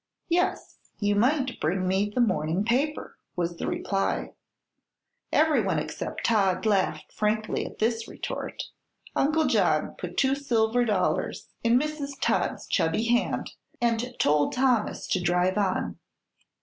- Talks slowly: Yes, slow, 130 wpm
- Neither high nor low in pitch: No, high, 220 Hz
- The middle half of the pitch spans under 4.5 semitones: No, average, 5.2 semitones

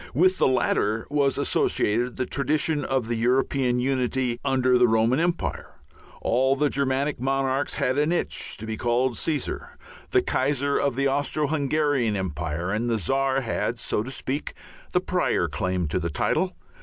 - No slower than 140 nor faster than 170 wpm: Yes, average, 165 wpm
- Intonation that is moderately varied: Yes, average, 3.3 semitones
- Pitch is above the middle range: No, low, 130 Hz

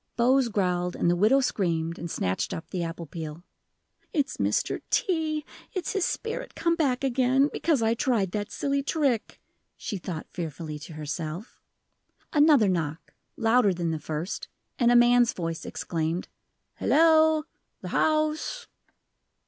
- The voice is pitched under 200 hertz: No, high, 225 Hz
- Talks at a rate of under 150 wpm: Yes, average, 140 wpm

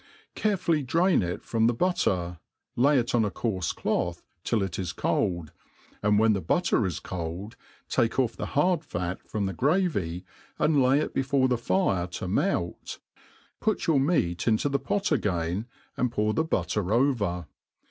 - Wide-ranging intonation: Yes, wide, 7.7 semitones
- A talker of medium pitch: No, low, 110 Hz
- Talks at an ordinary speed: Yes, average, 160 wpm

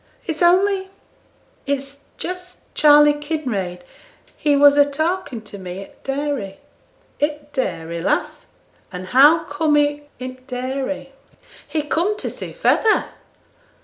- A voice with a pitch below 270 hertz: No, very high, 290 Hz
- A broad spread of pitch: No, average, 3.7 semitones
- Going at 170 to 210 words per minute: No, slow, 135 wpm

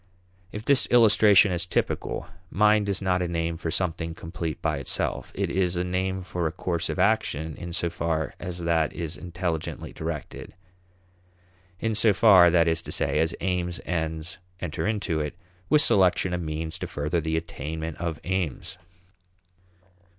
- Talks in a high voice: No, very low, 85 Hz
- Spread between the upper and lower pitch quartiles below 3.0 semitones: Yes, narrow, 2.5 semitones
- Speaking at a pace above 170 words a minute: No, average, 165 wpm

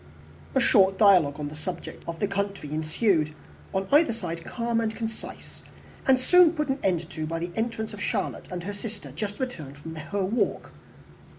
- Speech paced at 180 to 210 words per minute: Yes, average, 185 wpm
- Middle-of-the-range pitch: No, high, 195 Hz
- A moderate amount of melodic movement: No, wide, 5.7 semitones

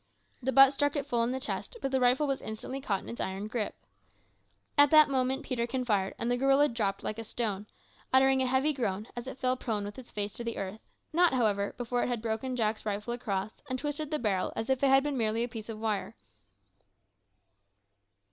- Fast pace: Yes, fast, 220 wpm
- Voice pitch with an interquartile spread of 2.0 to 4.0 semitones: Yes, average, 3.6 semitones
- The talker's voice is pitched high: Yes, high, 245 Hz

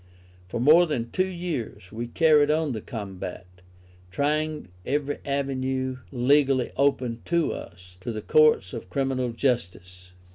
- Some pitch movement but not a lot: Yes, average, 4.8 semitones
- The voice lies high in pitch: No, low, 130 Hz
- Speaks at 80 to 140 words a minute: Yes, slow, 135 wpm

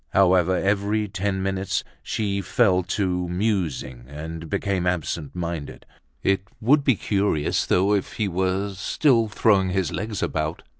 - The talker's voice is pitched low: Yes, very low, 95 Hz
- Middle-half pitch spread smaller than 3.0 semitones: Yes, narrow, 2.5 semitones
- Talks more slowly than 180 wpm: Yes, average, 140 wpm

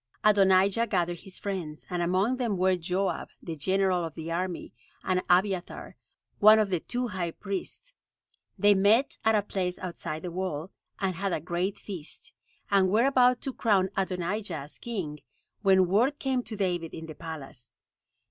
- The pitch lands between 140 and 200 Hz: Yes, high, 190 Hz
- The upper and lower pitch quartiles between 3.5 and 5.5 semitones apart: No, average, 3.0 semitones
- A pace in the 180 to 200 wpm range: No, average, 165 wpm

